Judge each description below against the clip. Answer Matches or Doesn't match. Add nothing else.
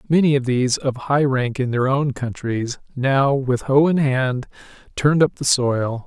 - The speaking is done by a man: Matches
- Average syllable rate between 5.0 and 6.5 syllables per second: Doesn't match